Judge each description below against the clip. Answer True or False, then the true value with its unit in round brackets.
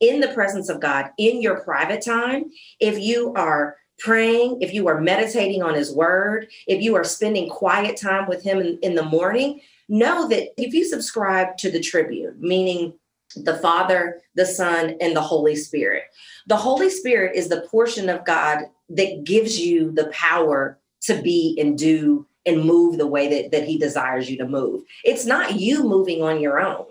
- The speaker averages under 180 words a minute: False (185 wpm)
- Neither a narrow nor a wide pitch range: False (5.7 semitones)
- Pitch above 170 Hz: True (185 Hz)